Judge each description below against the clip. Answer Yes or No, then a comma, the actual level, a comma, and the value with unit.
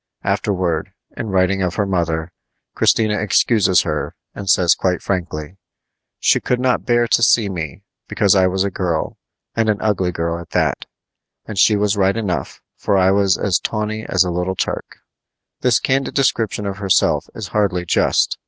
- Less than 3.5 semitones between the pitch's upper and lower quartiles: Yes, average, 3.0 semitones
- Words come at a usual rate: Yes, average, 170 wpm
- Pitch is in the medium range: No, very low, 95 Hz